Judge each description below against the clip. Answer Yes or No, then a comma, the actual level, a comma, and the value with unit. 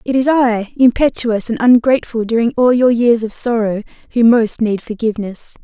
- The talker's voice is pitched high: Yes, high, 230 Hz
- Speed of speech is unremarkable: Yes, average, 150 wpm